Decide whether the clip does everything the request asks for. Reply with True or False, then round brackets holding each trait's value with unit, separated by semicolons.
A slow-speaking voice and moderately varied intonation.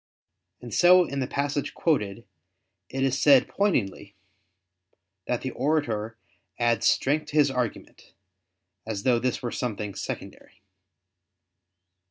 True (120 wpm; 3.9 semitones)